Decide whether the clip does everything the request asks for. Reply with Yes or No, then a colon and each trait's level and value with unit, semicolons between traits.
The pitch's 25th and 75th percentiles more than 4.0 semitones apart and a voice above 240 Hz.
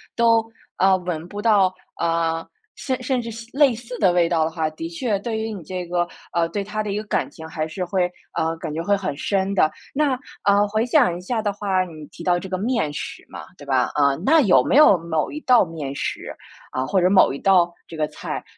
No: average, 5.0 semitones; medium, 185 Hz